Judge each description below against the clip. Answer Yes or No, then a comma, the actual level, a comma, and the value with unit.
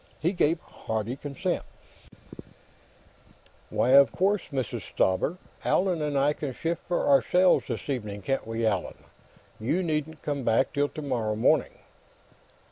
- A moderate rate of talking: No, slow, 130 wpm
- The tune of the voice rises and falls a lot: Yes, wide, 5.7 semitones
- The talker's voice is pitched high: No, medium, 140 Hz